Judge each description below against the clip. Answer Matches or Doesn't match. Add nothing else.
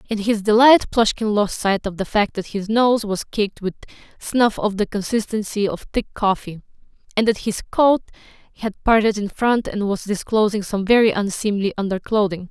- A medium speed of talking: Matches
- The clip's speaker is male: Doesn't match